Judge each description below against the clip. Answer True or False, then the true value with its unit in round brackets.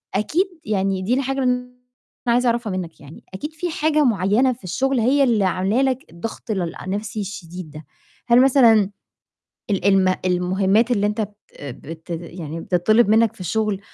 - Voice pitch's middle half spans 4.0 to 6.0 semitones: True (5.1 semitones)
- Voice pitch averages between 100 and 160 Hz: False (210 Hz)